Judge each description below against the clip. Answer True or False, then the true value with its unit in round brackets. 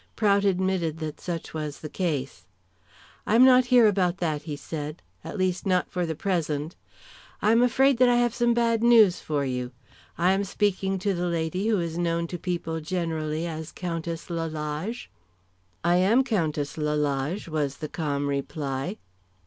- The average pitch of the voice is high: False (170 Hz)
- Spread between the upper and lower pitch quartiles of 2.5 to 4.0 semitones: False (4.5 semitones)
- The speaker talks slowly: False (165 wpm)